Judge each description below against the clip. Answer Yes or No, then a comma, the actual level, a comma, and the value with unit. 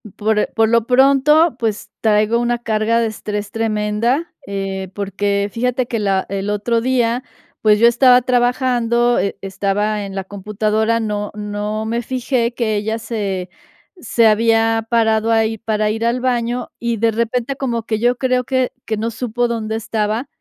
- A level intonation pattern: Yes, narrow, 2.3 semitones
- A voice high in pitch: Yes, high, 225 Hz